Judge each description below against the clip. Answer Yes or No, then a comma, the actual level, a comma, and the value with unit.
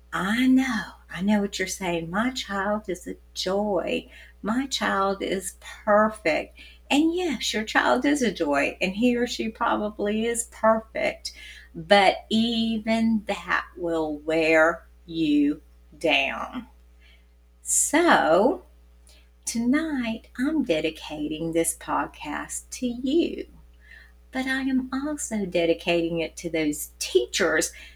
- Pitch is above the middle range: Yes, high, 195 Hz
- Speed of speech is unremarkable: No, slow, 115 wpm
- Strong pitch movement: Yes, wide, 7.5 semitones